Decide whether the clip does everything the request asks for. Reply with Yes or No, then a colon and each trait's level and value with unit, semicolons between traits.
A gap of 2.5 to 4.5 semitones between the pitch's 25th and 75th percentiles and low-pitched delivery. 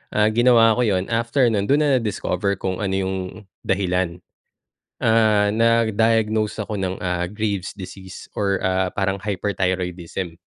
Yes: average, 3.0 semitones; low, 100 Hz